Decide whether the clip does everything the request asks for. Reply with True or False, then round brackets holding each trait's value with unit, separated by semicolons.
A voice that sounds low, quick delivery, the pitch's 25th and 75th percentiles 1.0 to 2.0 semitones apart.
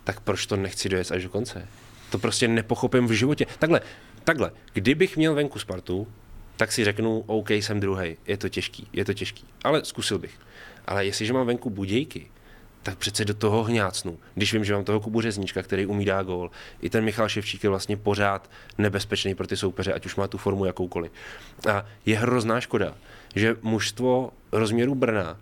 False (105 Hz; 185 wpm; 2.7 semitones)